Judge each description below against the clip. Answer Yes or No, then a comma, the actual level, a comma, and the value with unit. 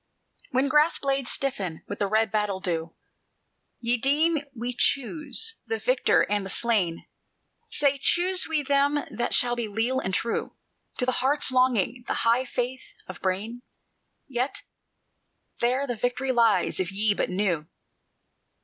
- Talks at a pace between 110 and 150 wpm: Yes, average, 145 wpm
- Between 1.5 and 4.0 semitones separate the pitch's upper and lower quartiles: No, average, 4.8 semitones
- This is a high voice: Yes, high, 245 Hz